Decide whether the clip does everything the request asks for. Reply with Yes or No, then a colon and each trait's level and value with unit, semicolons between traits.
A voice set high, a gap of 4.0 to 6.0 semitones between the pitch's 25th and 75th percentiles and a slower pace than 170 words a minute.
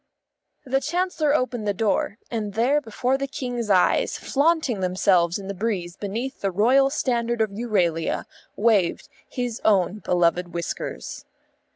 Yes: high, 220 Hz; average, 5.1 semitones; average, 140 wpm